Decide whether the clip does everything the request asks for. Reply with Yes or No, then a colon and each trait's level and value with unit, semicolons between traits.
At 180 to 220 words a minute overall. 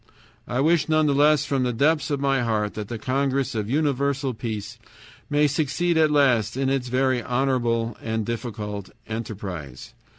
No: average, 165 wpm